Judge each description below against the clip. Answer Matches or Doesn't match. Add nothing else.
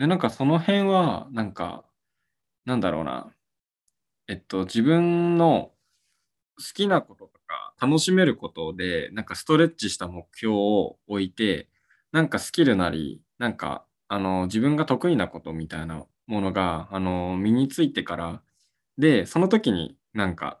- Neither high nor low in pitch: Doesn't match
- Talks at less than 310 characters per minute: Matches